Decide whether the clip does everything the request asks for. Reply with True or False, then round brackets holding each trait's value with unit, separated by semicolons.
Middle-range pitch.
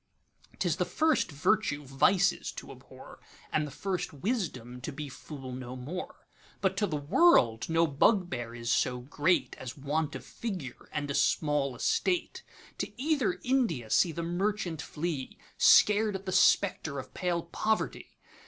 True (160 Hz)